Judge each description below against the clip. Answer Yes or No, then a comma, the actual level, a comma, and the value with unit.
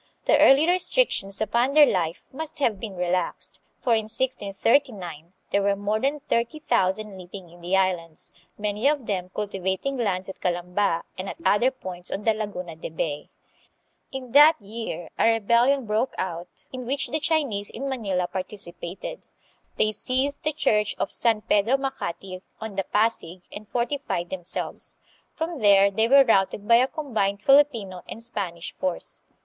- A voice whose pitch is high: Yes, high, 210 Hz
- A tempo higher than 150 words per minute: Yes, average, 160 wpm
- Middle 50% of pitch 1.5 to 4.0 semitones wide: No, wide, 5.5 semitones